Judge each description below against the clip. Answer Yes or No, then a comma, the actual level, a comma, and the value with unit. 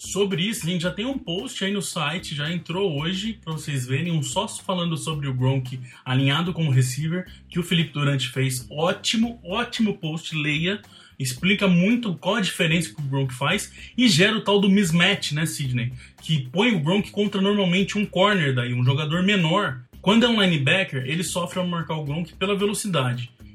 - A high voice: No, medium, 175 Hz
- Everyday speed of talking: No, fast, 195 wpm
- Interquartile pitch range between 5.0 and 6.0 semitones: Yes, average, 5.3 semitones